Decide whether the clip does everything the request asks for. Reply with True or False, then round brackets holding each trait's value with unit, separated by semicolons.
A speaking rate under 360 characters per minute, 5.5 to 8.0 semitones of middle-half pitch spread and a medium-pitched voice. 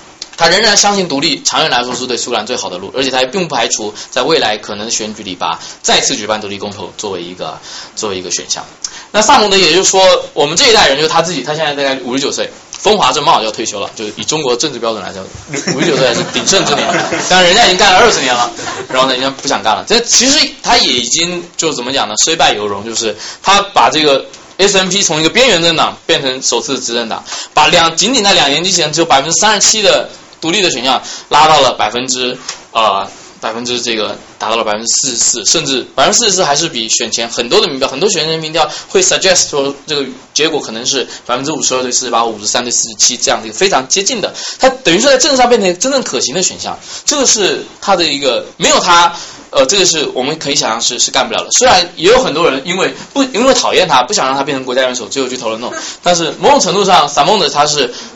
False (385 characters per minute; 7.6 semitones; 150 Hz)